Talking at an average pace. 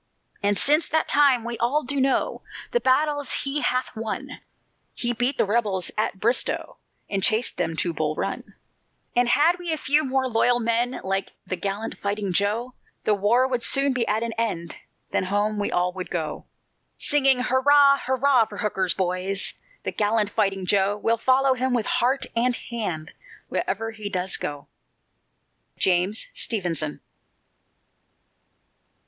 Yes: average, 155 wpm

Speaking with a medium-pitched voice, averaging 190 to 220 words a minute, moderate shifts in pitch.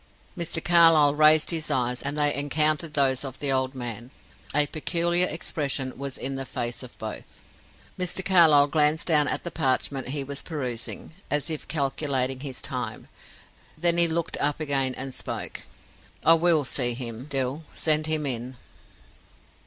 No: medium, 145 Hz; average, 160 wpm; average, 3.2 semitones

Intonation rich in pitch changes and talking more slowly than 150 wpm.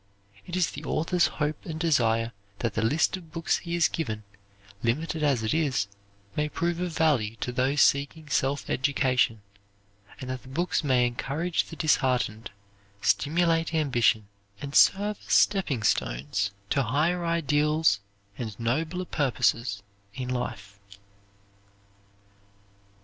Yes: wide, 5.7 semitones; slow, 135 wpm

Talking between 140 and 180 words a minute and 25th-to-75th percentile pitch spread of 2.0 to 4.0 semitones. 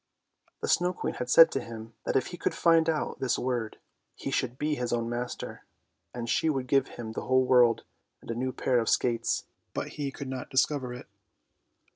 No: fast, 205 wpm; narrow, 2.5 semitones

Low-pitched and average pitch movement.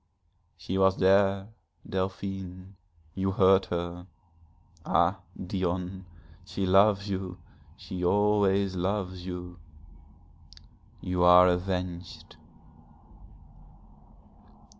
No: very low, 95 Hz; narrow, 1.3 semitones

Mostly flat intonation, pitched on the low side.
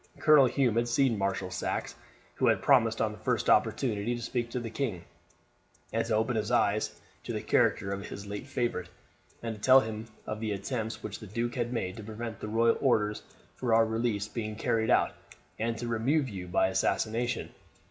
Yes: narrow, 2.3 semitones; low, 110 Hz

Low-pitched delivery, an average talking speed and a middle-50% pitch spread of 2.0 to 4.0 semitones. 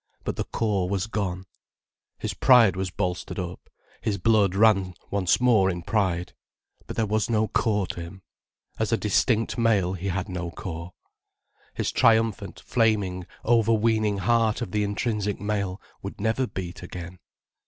Yes: low, 100 Hz; average, 155 wpm; average, 3.3 semitones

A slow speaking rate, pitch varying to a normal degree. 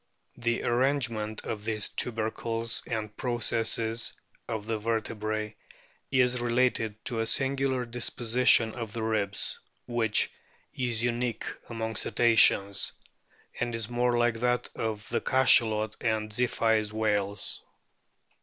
No: slow, 115 wpm; narrow, 1.8 semitones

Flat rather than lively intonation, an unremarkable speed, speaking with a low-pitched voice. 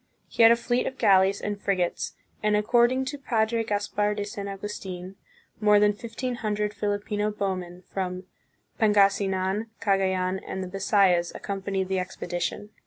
No: narrow, 1.9 semitones; average, 150 wpm; high, 205 Hz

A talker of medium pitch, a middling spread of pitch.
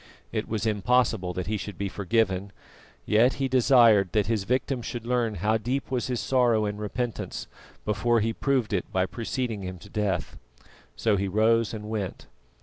No: low, 110 Hz; average, 3.1 semitones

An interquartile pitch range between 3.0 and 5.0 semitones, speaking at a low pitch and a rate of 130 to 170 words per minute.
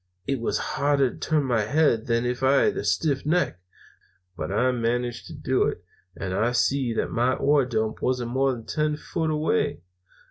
No: average, 3.4 semitones; low, 125 Hz; average, 190 wpm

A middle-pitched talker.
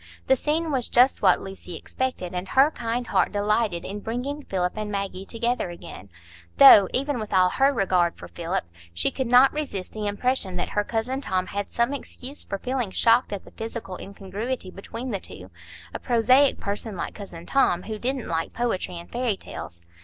No: high, 210 Hz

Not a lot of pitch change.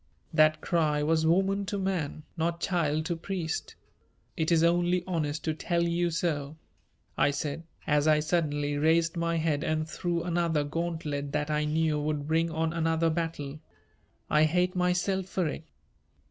Yes: narrow, 2.1 semitones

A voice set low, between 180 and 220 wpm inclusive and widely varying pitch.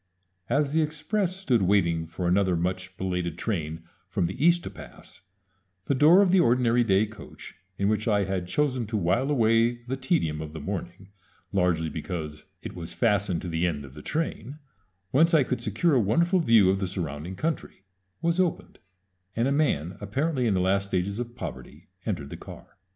Yes: low, 105 Hz; average, 190 wpm; wide, 7.3 semitones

